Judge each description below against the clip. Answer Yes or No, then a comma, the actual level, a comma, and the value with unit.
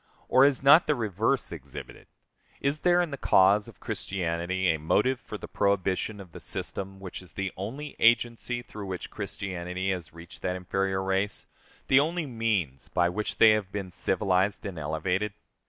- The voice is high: No, very low, 95 Hz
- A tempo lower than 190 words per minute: Yes, average, 170 wpm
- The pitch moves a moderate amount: Yes, average, 4.0 semitones